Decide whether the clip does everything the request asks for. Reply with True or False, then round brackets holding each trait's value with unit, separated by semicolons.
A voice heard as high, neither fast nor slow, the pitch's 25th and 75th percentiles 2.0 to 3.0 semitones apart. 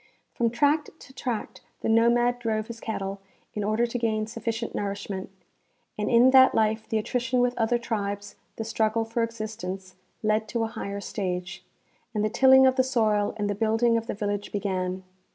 True (220 Hz; 180 wpm; 2.5 semitones)